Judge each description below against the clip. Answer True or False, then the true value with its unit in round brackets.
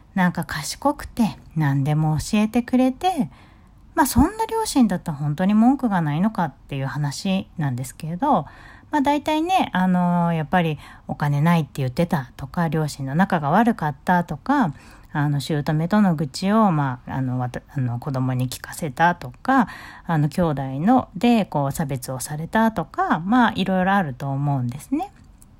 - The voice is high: False (170 Hz)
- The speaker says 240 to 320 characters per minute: True (315 characters per minute)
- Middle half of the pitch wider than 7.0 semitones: True (7.5 semitones)